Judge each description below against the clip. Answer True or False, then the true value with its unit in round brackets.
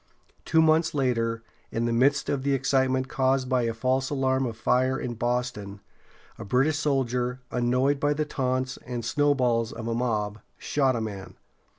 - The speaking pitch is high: False (130 Hz)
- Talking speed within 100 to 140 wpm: False (170 wpm)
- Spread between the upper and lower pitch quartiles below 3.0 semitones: True (2.5 semitones)